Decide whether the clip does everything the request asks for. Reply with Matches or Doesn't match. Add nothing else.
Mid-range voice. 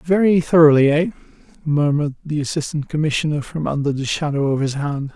Matches